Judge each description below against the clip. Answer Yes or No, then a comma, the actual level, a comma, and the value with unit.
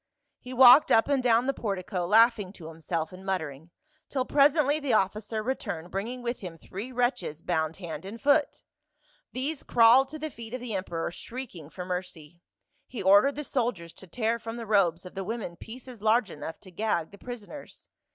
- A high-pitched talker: Yes, high, 220 Hz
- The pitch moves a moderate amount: No, wide, 5.7 semitones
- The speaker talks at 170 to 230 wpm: Yes, average, 185 wpm